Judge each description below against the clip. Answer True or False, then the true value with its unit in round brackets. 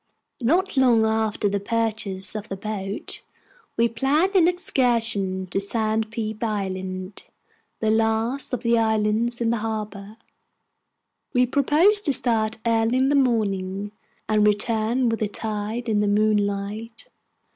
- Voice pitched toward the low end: False (220 Hz)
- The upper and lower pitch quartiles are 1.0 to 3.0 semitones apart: True (2.4 semitones)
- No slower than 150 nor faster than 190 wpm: False (135 wpm)